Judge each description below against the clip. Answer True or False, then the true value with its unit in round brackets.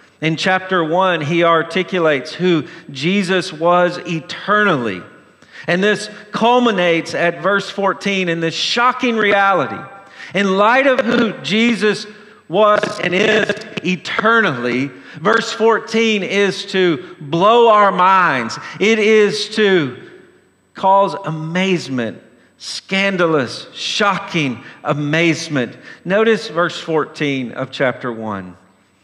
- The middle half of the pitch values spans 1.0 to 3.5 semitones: False (4.5 semitones)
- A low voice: False (185 Hz)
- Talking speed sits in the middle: False (100 wpm)